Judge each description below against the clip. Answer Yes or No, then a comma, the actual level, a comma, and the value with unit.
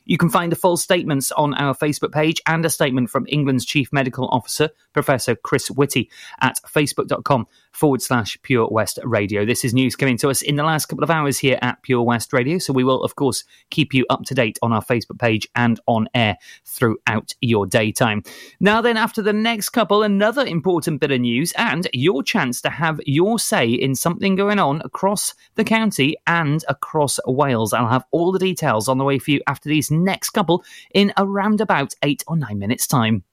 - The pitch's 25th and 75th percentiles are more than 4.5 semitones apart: Yes, average, 5.1 semitones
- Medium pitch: Yes, medium, 145 Hz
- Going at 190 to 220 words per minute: Yes, fast, 205 wpm